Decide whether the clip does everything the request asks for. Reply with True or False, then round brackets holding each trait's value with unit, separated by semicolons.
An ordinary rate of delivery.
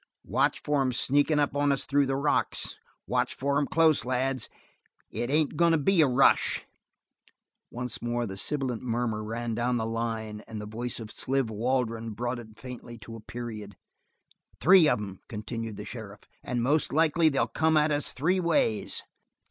True (180 wpm)